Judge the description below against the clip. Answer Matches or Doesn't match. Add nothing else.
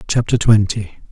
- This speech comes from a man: Matches